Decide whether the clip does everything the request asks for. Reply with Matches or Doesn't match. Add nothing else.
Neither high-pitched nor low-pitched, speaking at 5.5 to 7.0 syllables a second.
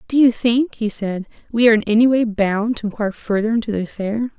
Doesn't match